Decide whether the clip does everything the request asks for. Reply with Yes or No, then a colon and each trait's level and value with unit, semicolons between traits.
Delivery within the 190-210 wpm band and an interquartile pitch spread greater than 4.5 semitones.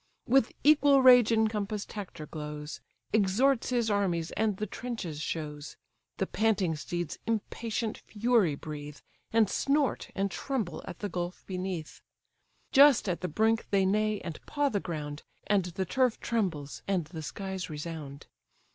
No: average, 145 wpm; wide, 5.6 semitones